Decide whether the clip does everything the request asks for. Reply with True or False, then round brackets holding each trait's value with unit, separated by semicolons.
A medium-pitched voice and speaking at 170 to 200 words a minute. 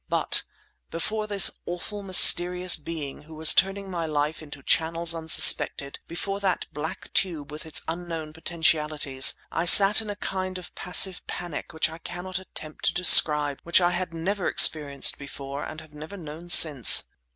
False (165 Hz; 160 wpm)